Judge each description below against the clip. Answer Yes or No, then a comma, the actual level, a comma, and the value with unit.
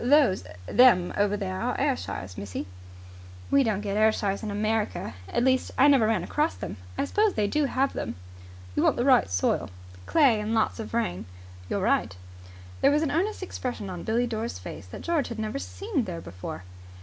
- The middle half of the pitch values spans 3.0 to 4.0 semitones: No, wide, 5.6 semitones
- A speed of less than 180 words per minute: No, average, 190 wpm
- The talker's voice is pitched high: Yes, high, 220 Hz